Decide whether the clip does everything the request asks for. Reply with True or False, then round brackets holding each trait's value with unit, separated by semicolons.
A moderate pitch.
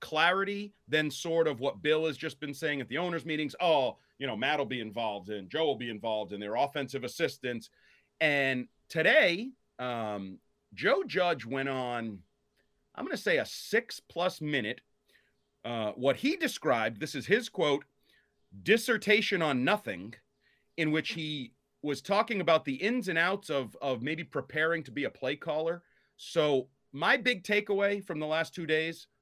True (155 Hz)